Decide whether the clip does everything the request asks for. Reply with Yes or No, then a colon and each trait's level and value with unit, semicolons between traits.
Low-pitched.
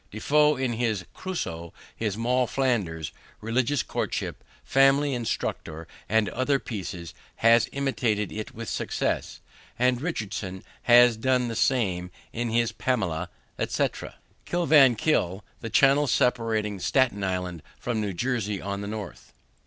Yes: low, 115 Hz